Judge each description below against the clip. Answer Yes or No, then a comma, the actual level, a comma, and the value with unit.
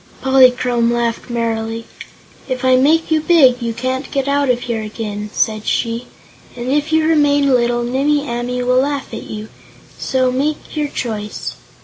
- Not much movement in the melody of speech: No, average, 3.1 semitones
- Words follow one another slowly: No, average, 160 wpm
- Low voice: No, very high, 250 Hz